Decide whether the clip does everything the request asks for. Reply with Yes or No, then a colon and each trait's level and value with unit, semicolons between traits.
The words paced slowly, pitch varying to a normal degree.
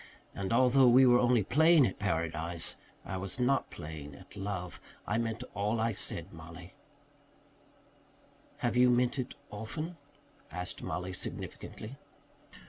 No: slow, 130 wpm; wide, 5.7 semitones